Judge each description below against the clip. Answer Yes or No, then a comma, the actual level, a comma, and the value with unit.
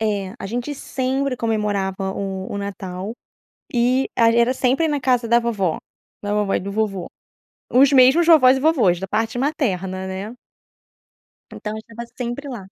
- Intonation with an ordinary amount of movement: Yes, average, 4.7 semitones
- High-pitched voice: Yes, high, 230 Hz